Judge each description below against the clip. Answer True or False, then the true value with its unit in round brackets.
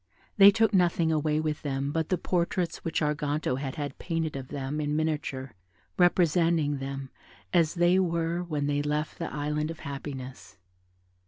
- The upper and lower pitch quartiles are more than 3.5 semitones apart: False (2.7 semitones)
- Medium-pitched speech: True (155 Hz)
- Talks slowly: False (160 wpm)